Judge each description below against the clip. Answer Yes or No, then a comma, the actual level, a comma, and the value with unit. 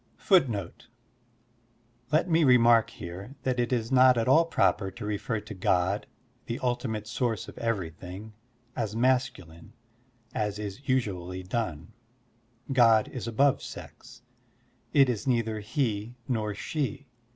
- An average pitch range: Yes, average, 3.8 semitones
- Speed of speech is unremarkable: No, slow, 130 wpm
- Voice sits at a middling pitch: No, low, 115 Hz